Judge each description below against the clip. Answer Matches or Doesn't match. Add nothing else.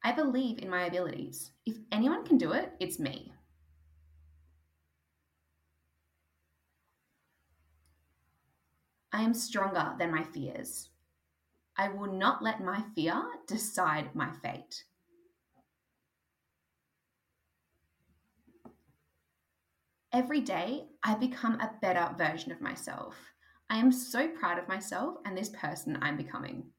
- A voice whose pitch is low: Doesn't match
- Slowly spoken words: Matches